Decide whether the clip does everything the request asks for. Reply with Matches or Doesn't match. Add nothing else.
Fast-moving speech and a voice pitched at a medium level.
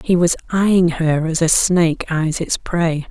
Doesn't match